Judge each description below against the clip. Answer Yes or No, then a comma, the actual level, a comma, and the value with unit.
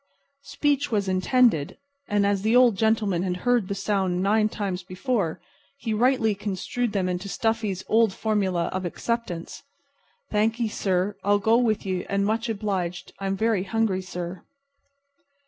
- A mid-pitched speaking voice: No, high, 205 Hz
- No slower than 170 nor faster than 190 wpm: No, average, 145 wpm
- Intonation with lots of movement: No, average, 3.2 semitones